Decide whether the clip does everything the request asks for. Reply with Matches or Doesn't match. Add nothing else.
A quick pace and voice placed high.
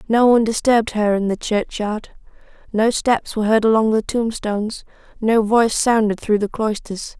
Doesn't match